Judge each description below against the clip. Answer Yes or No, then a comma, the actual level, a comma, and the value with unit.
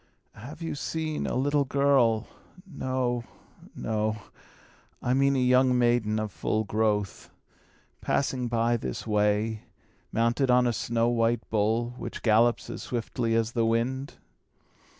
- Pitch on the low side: Yes, low, 120 Hz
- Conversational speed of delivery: No, slow, 130 wpm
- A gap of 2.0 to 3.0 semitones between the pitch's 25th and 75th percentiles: Yes, average, 2.7 semitones